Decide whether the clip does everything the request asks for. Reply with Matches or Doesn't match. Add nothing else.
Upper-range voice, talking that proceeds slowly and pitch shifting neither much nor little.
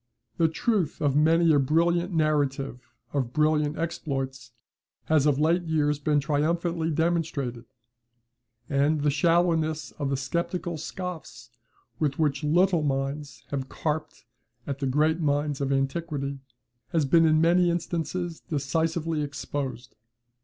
Doesn't match